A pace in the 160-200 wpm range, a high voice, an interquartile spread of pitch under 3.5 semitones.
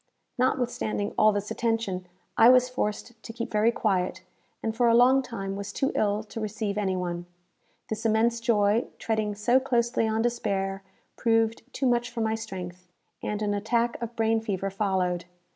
Yes: average, 170 wpm; high, 220 Hz; narrow, 2.6 semitones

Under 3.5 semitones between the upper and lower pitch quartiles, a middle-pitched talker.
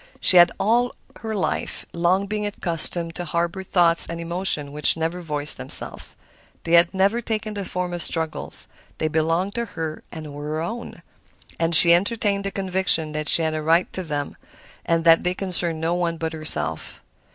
Yes: average, 2.9 semitones; medium, 170 Hz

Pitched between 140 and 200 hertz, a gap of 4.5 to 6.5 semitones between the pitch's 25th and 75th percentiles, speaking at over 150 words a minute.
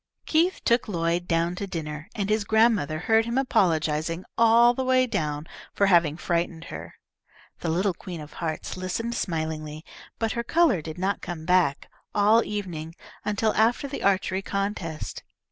Yes: medium, 185 Hz; wide, 5.4 semitones; average, 160 wpm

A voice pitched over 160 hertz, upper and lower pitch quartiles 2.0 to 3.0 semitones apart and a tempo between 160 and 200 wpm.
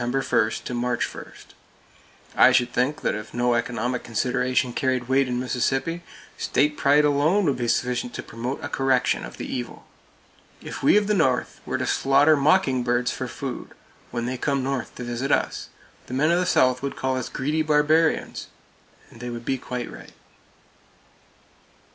No: low, 130 Hz; average, 2.7 semitones; average, 170 wpm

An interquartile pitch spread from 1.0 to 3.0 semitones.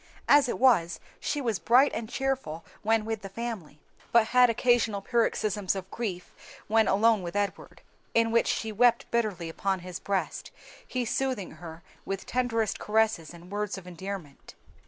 No: average, 3.8 semitones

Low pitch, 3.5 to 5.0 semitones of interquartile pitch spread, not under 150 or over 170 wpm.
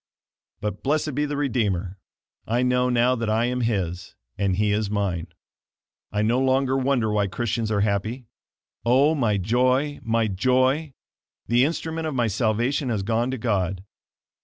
Yes: low, 120 Hz; average, 3.9 semitones; average, 160 wpm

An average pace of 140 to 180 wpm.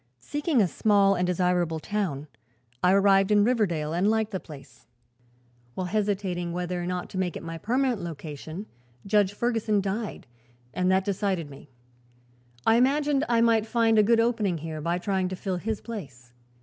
Yes: average, 170 wpm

